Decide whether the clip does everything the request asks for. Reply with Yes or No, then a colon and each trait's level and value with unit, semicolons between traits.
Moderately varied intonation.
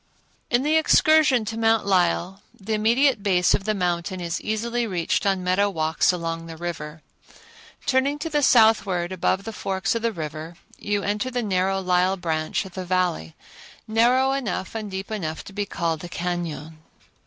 Yes: average, 4.4 semitones